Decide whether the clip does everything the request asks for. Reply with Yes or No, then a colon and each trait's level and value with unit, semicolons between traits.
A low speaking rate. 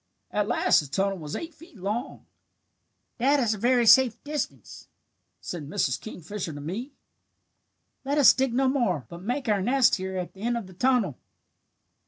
No: average, 175 wpm